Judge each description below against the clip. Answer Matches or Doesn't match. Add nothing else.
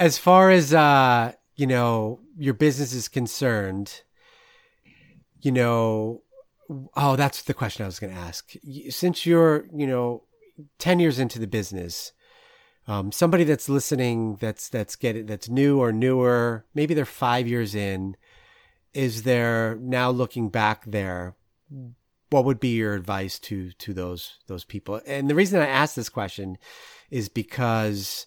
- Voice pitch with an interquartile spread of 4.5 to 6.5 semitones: Matches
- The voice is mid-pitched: Doesn't match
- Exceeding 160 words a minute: Doesn't match